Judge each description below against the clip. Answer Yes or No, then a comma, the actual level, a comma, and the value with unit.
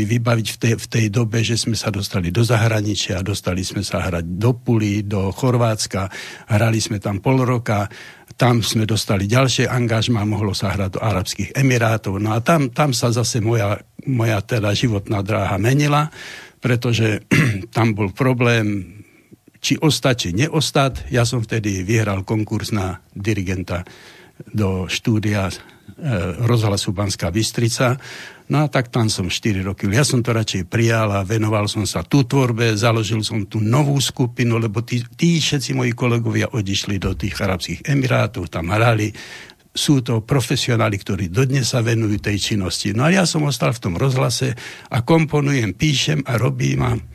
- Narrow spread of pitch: No, average, 3.5 semitones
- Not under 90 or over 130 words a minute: No, average, 160 wpm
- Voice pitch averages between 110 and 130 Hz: Yes, low, 115 Hz